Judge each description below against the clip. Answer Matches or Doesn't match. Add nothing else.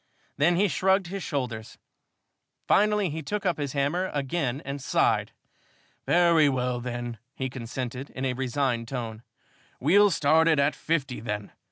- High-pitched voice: Doesn't match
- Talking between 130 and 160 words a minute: Matches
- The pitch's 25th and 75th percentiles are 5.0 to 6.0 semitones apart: Matches